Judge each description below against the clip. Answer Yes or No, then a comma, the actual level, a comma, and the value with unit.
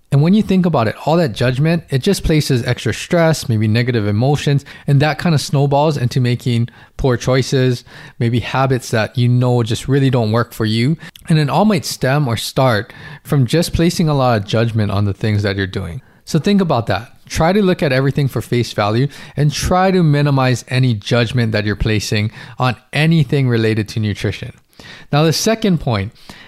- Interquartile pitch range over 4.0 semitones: Yes, average, 4.6 semitones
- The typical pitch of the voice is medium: No, low, 130 Hz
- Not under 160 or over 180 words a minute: No, average, 195 wpm